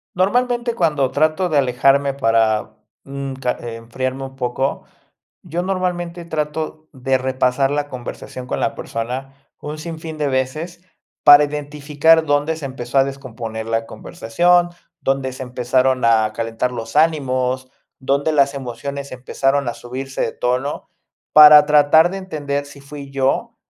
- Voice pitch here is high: No, medium, 140 Hz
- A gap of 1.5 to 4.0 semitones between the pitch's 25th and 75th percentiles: Yes, average, 3.1 semitones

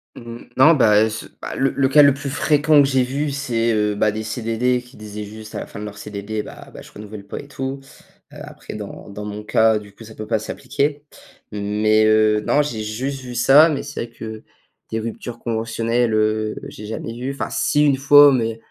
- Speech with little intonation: No, average, 3.9 semitones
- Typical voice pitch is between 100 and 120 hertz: Yes, low, 115 Hz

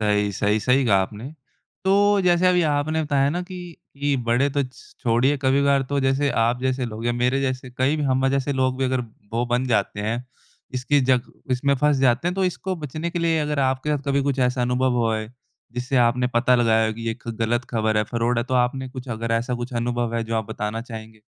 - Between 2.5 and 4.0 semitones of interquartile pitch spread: Yes, average, 3.1 semitones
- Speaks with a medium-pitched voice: No, low, 130 Hz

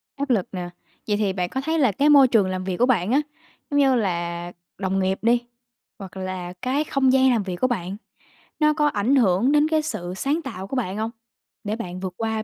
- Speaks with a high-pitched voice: Yes, high, 220 Hz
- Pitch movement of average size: No, wide, 6.2 semitones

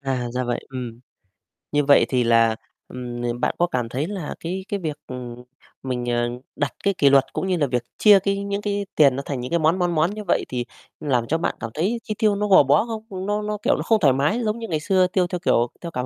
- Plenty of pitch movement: Yes, wide, 7.8 semitones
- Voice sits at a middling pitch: Yes, medium, 155 Hz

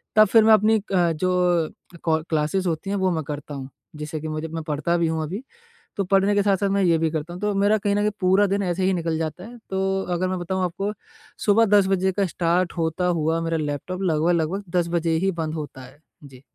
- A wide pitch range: No, average, 3.3 semitones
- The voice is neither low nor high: Yes, medium, 175 Hz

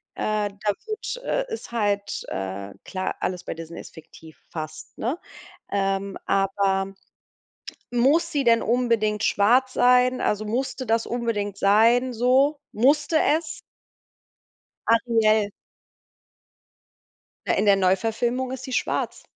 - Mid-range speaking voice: No, high, 225 Hz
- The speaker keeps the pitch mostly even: No, average, 4.2 semitones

